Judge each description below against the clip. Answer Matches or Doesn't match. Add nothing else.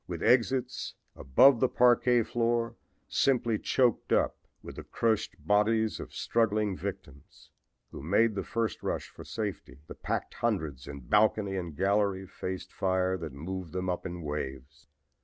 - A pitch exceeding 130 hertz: Doesn't match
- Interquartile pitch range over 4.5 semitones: Matches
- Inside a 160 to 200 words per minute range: Doesn't match